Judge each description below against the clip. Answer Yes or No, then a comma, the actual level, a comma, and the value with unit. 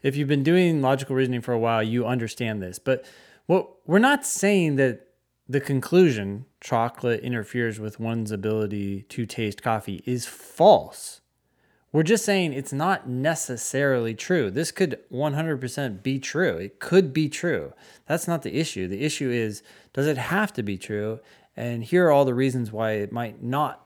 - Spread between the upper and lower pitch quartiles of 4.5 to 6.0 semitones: Yes, average, 5.3 semitones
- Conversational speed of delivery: Yes, average, 175 wpm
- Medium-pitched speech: No, low, 130 Hz